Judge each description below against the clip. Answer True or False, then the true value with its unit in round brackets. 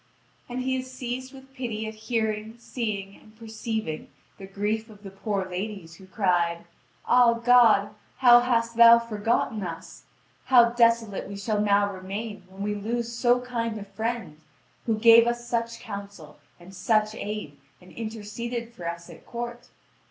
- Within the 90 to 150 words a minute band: False (160 wpm)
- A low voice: False (220 Hz)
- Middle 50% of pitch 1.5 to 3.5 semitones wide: True (2.8 semitones)